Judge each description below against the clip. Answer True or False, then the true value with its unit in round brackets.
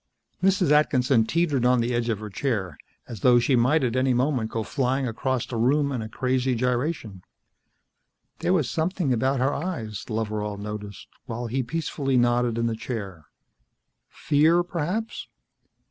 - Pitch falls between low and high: False (125 Hz)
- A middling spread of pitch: True (3.9 semitones)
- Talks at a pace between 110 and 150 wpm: False (160 wpm)